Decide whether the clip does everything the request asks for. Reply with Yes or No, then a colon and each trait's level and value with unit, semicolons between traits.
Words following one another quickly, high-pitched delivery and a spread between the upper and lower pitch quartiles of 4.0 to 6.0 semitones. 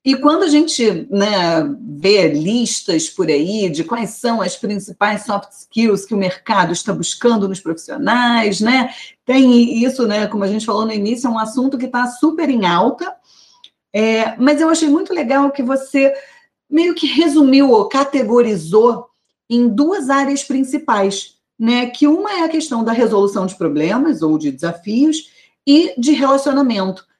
No: average, 165 wpm; high, 240 Hz; wide, 5.5 semitones